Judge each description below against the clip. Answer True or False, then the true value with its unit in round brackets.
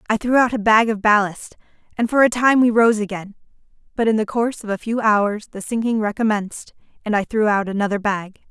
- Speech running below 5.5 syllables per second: False (5.8 syllables/s)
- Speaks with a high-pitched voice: True (215 Hz)